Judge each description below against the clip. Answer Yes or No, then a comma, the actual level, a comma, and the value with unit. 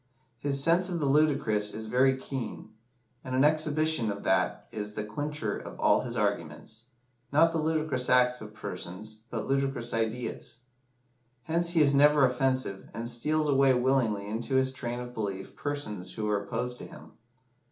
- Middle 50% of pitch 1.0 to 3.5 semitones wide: No, average, 4.9 semitones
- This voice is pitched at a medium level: No, low, 125 Hz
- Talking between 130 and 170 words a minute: Yes, average, 165 wpm